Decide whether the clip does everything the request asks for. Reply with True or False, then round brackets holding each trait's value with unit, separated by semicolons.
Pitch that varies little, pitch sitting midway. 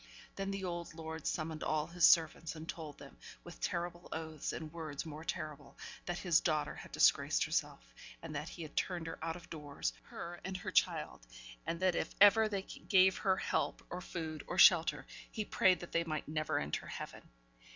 True (2.3 semitones; 165 Hz)